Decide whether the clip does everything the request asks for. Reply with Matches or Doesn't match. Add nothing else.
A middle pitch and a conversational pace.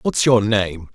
Doesn't match